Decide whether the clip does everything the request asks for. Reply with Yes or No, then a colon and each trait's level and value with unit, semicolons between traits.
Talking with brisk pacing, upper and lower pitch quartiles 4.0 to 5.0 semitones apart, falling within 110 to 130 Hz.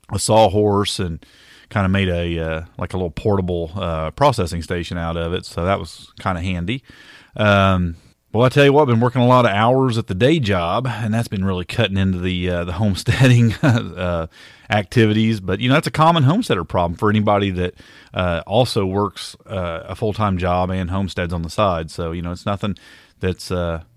No: fast, 210 wpm; average, 4.3 semitones; very low, 95 Hz